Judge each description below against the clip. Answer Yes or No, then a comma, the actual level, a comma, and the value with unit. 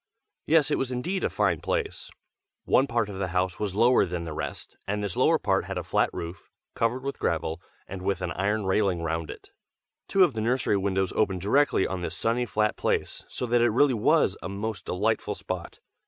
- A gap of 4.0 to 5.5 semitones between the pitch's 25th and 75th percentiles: Yes, average, 4.7 semitones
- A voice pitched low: Yes, low, 105 Hz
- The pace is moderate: No, fast, 210 wpm